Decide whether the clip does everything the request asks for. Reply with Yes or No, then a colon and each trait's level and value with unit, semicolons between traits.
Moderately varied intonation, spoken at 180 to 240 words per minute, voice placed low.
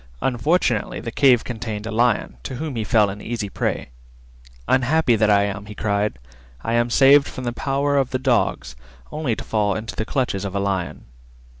Yes: average, 4.0 semitones; average, 190 wpm; low, 115 Hz